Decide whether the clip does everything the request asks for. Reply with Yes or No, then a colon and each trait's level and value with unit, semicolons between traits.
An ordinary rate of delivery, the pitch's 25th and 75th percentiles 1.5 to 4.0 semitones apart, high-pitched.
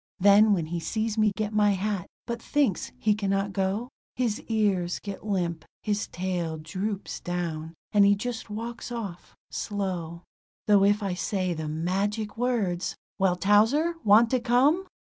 Yes: average, 155 wpm; average, 3.3 semitones; high, 200 Hz